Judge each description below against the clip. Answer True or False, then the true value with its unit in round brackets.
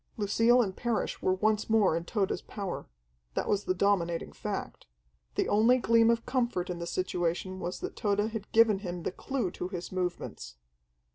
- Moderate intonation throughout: True (3.9 semitones)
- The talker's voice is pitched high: True (200 Hz)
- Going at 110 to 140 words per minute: False (180 wpm)